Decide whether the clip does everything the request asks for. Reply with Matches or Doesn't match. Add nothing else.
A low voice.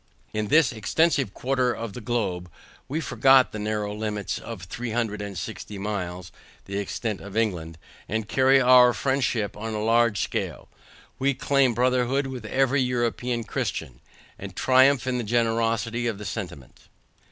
Matches